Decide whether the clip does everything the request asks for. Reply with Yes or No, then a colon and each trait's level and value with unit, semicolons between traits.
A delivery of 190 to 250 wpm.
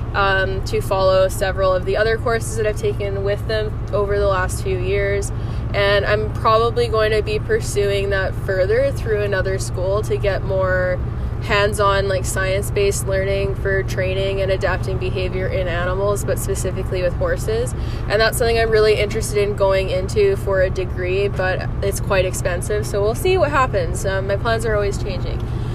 No: average, 180 wpm